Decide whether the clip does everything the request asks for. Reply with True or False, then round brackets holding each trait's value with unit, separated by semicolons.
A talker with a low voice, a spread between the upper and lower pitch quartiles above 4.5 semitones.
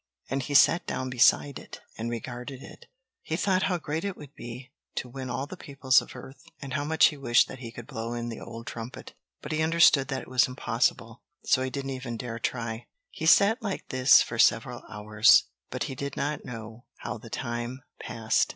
False (130 Hz; 3.3 semitones)